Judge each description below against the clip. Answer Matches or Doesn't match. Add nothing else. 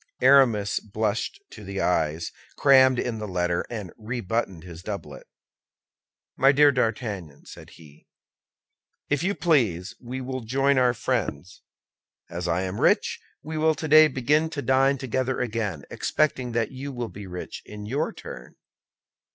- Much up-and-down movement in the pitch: Matches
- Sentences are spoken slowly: Doesn't match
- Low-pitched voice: Matches